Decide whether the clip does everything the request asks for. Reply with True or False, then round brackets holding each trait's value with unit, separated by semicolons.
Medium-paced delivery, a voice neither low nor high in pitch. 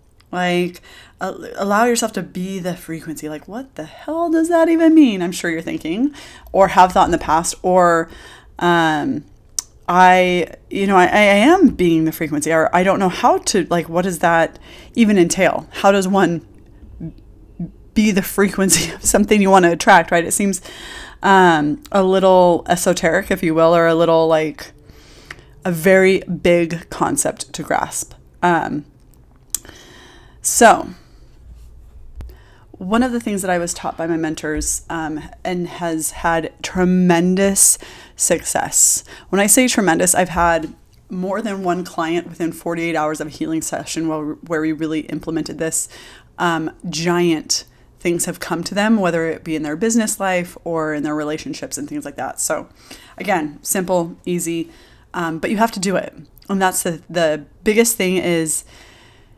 True (165 wpm; 175 Hz)